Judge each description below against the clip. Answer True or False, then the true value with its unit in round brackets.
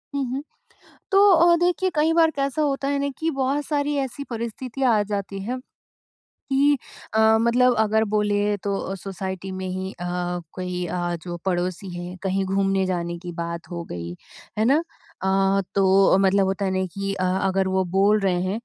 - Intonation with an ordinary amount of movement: False (6.0 semitones)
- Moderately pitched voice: False (195 Hz)